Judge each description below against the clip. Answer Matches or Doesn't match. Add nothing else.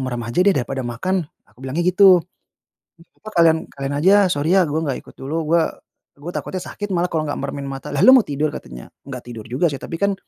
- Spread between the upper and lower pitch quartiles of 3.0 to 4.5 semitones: Doesn't match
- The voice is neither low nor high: Matches